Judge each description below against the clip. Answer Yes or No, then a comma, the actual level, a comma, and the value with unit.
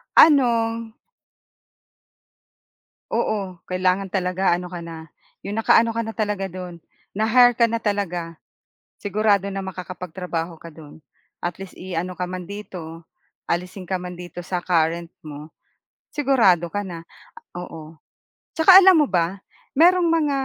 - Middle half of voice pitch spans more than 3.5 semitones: Yes, average, 4.3 semitones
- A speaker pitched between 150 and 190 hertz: Yes, medium, 185 Hz